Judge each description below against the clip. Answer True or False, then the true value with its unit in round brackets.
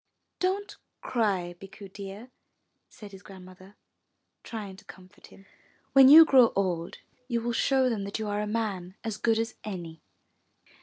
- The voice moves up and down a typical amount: True (3.4 semitones)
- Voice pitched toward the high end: True (205 Hz)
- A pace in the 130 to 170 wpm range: True (155 wpm)